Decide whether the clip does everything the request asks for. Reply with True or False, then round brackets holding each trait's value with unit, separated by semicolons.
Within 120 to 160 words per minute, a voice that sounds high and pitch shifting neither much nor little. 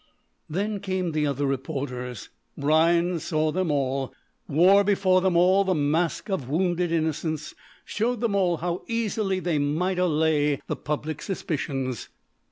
False (140 wpm; 165 Hz; 4.2 semitones)